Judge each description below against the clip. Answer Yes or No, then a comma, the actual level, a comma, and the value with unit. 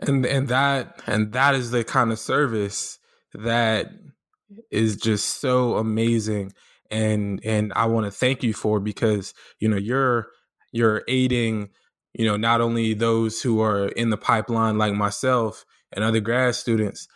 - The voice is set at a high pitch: No, low, 115 Hz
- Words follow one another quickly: No, average, 160 wpm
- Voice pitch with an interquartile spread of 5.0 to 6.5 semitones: No, narrow, 2.4 semitones